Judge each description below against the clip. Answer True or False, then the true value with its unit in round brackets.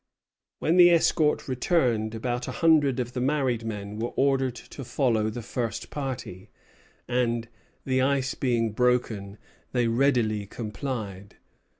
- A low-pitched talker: True (125 Hz)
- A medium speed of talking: False (130 wpm)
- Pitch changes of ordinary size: True (3.4 semitones)